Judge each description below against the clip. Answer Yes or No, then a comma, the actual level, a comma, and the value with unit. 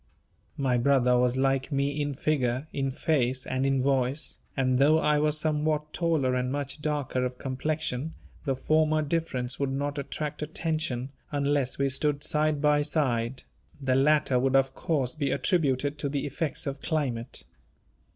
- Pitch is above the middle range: No, medium, 140 Hz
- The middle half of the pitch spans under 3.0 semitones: Yes, narrow, 2.6 semitones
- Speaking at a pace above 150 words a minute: Yes, average, 160 wpm